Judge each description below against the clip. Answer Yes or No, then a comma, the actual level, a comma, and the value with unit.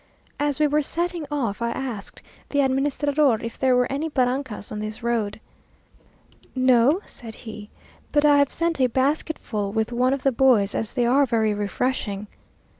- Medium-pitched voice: No, very high, 255 Hz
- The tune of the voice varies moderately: Yes, average, 4.4 semitones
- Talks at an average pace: Yes, average, 170 wpm